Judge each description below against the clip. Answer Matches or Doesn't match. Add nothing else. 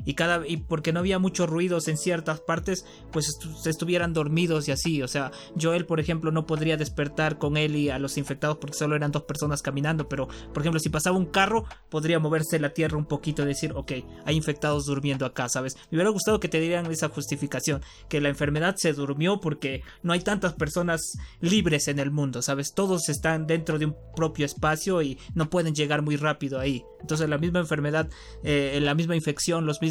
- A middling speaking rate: Doesn't match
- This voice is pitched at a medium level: Matches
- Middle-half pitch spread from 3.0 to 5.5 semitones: Doesn't match